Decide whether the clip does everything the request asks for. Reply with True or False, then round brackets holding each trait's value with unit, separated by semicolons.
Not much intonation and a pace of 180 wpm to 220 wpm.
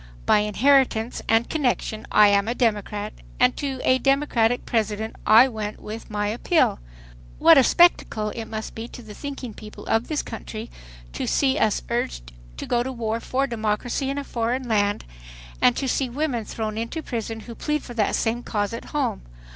False (3.3 semitones; 185 wpm)